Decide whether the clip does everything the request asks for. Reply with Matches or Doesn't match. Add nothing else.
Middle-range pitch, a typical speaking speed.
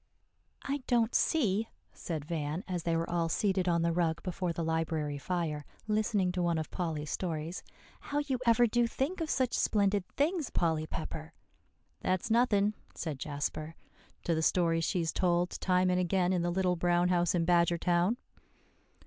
Matches